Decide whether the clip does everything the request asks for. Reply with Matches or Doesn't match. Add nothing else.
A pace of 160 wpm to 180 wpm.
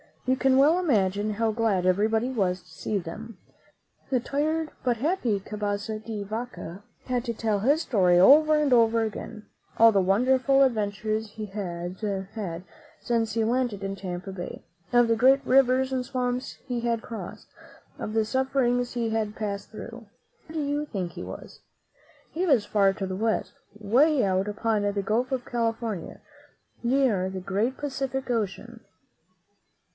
Matches